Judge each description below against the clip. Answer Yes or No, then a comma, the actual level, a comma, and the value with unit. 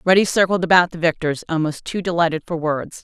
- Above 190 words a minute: Yes, average, 200 wpm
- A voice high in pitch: No, medium, 170 Hz